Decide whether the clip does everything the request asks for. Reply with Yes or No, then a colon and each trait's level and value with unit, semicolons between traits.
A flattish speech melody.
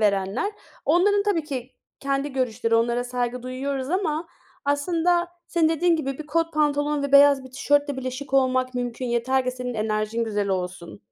No: average, 3.6 semitones